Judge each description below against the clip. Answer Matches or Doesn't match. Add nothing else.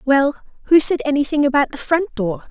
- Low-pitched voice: Doesn't match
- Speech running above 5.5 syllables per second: Matches